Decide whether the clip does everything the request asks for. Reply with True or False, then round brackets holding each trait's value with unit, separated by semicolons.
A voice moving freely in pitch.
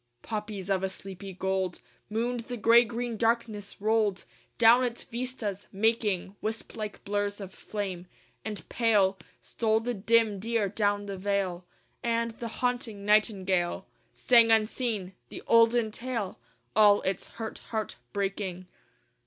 False (2.8 semitones)